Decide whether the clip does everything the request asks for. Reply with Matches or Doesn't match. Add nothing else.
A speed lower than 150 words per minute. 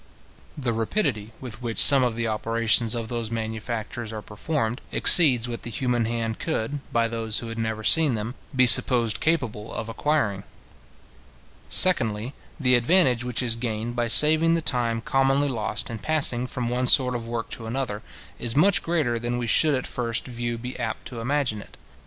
Doesn't match